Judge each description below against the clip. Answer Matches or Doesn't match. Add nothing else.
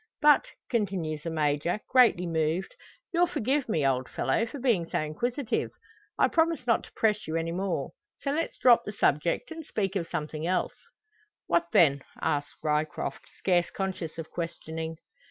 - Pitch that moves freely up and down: Matches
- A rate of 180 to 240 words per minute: Doesn't match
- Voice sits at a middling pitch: Matches